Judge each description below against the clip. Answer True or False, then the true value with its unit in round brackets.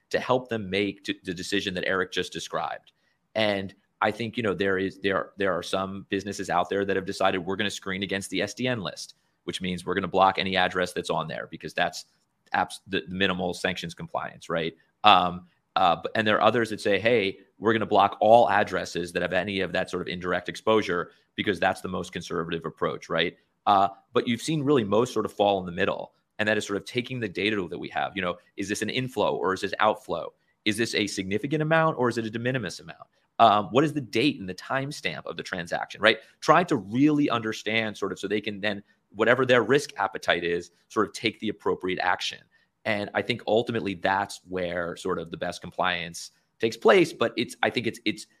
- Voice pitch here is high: False (100 Hz)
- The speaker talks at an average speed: False (230 wpm)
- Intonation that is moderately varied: True (3.2 semitones)